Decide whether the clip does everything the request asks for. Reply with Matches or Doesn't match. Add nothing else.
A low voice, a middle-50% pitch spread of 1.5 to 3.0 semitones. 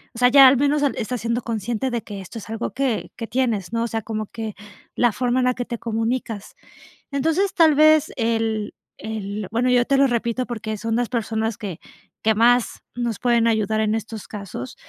Doesn't match